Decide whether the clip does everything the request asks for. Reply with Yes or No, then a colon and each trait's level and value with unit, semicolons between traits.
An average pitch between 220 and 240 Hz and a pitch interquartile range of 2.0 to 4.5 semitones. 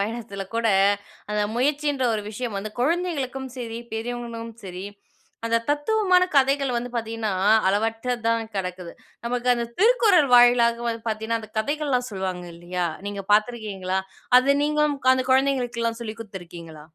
Yes: high, 230 Hz; average, 3.8 semitones